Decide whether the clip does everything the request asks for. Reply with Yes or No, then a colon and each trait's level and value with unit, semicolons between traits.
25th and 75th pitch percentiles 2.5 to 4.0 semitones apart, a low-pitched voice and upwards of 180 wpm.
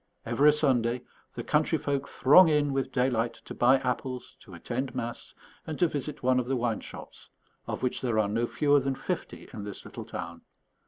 Yes: average, 3.0 semitones; low, 130 Hz; average, 195 wpm